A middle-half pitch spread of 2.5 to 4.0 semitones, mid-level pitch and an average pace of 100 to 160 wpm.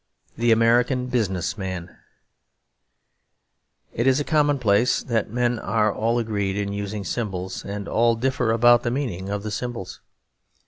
No: average, 3.2 semitones; low, 115 Hz; average, 140 wpm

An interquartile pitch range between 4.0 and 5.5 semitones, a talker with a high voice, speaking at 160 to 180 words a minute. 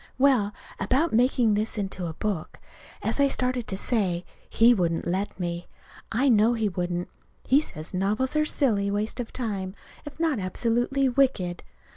Yes: average, 5.2 semitones; high, 215 Hz; average, 165 wpm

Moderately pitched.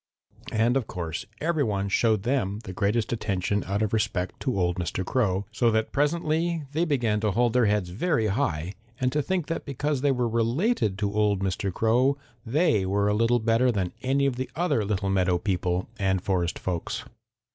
No: low, 110 Hz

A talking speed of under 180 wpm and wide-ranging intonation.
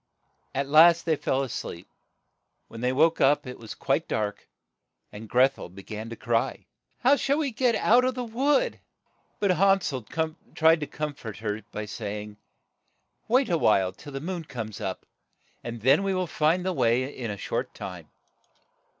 No: average, 195 wpm; wide, 8.7 semitones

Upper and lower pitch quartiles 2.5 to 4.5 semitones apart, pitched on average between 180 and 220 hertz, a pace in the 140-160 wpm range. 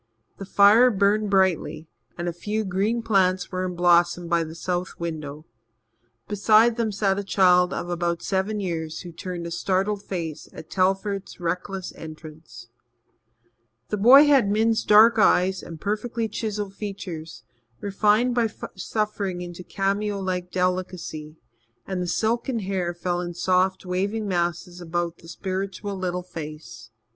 Yes: average, 3.0 semitones; medium, 185 Hz; average, 145 wpm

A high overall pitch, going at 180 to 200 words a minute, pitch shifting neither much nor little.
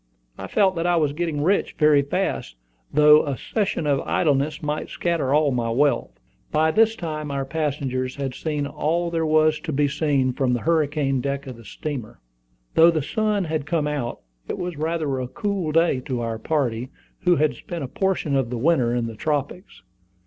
No: medium, 150 Hz; average, 190 wpm; average, 3.4 semitones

